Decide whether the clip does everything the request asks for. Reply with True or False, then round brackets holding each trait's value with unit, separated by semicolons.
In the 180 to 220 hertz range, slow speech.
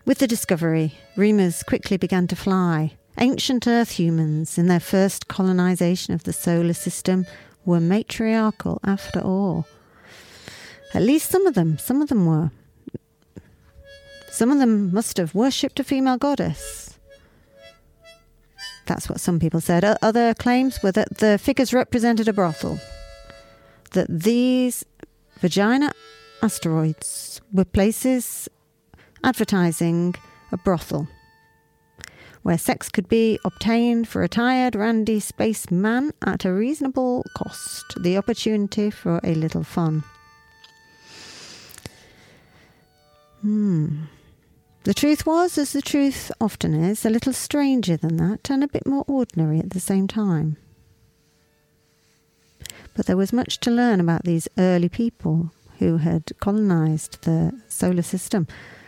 True (190 Hz; 125 wpm)